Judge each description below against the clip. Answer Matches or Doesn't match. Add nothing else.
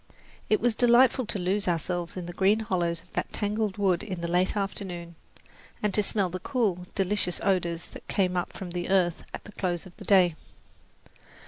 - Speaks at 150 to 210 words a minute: Matches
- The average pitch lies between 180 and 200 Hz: Matches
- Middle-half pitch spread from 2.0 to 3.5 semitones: Matches